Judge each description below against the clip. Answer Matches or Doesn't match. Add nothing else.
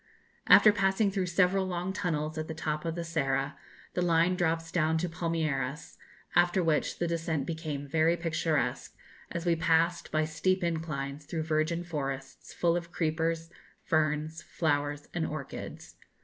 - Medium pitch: Matches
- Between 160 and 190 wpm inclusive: Doesn't match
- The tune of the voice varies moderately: Doesn't match